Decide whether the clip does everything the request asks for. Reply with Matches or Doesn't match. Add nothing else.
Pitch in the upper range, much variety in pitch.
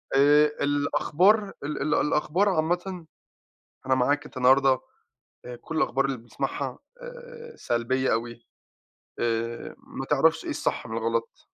Doesn't match